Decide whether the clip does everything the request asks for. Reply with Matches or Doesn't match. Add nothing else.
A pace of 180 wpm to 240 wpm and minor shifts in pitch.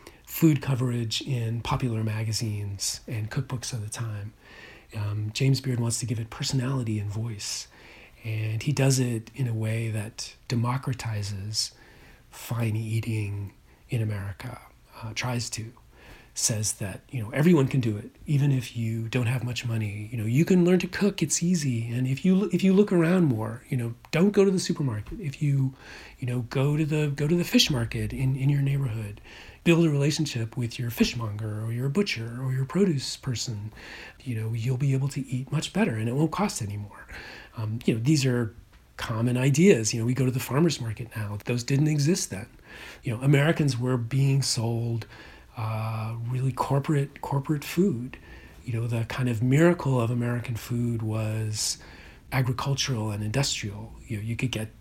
Doesn't match